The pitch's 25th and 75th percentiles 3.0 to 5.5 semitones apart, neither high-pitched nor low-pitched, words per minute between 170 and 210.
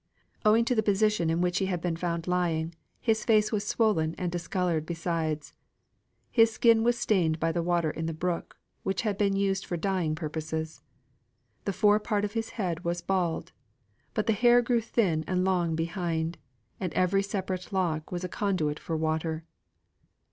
Yes: average, 4.0 semitones; medium, 180 Hz; average, 175 wpm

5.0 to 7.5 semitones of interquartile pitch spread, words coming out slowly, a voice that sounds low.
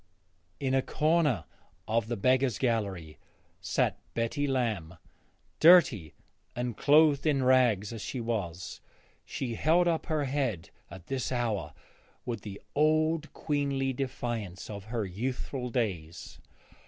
Yes: wide, 5.4 semitones; slow, 125 wpm; low, 120 Hz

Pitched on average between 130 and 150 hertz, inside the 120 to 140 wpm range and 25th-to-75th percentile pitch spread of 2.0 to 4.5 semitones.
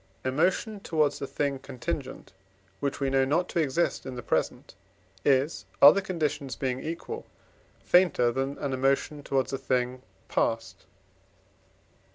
Yes: medium, 140 Hz; slow, 135 wpm; average, 3.3 semitones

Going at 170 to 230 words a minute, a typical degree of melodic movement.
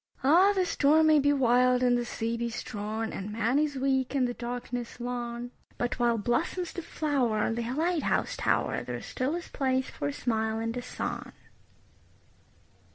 Yes: average, 180 wpm; average, 3.4 semitones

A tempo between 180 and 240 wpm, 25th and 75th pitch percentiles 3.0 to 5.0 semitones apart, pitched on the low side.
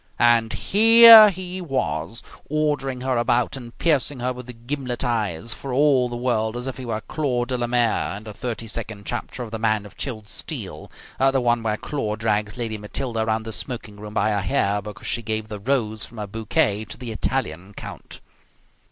Yes: average, 190 wpm; average, 3.4 semitones; low, 115 Hz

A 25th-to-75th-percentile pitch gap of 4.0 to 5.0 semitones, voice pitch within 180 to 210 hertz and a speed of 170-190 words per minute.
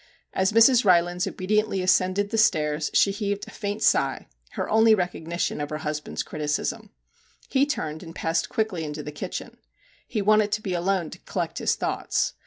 Yes: average, 4.7 semitones; medium, 185 Hz; average, 180 wpm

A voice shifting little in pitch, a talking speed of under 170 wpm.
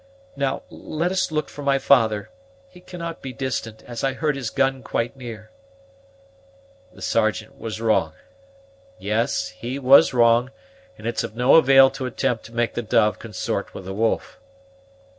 No: average, 3.5 semitones; average, 160 wpm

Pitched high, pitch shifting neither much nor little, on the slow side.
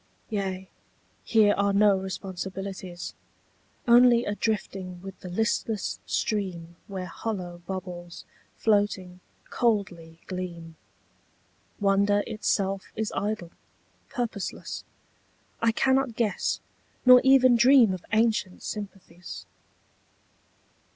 Yes: high, 200 Hz; average, 3.2 semitones; slow, 90 wpm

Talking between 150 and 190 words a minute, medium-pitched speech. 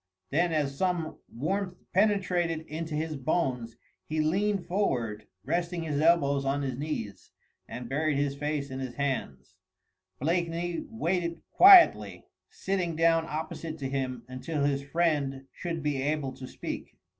No: average, 140 wpm; medium, 155 Hz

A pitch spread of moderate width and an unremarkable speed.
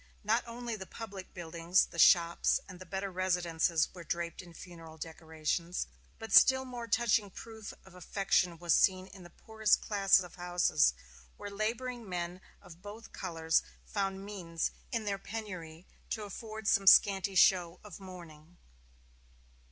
Yes: average, 3.5 semitones; average, 150 wpm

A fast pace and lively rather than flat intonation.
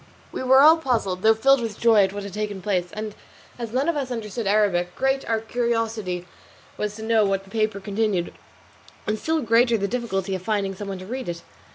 No: fast, 215 wpm; average, 3.3 semitones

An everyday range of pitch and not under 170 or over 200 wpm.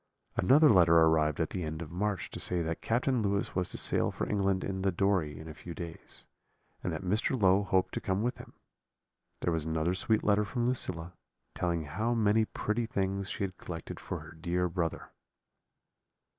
Yes: average, 3.8 semitones; average, 195 wpm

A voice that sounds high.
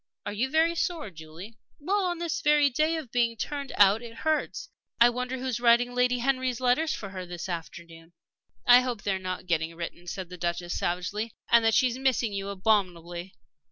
Yes: high, 230 Hz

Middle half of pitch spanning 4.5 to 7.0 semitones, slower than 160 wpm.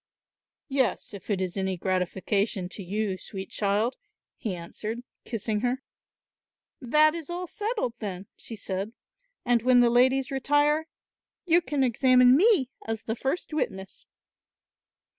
Yes: wide, 5.4 semitones; slow, 135 wpm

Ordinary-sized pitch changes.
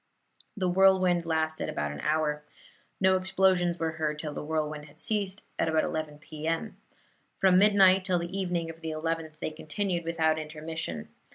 Yes: average, 3.0 semitones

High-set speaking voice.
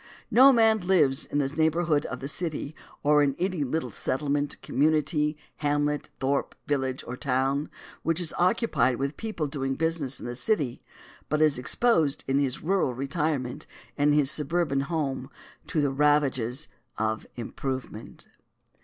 No: medium, 145 Hz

